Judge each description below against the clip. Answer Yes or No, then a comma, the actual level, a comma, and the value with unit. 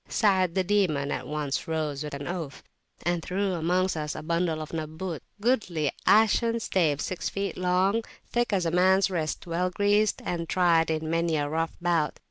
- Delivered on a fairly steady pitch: No, average, 3.2 semitones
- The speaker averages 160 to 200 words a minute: Yes, average, 180 wpm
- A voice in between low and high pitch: Yes, medium, 175 Hz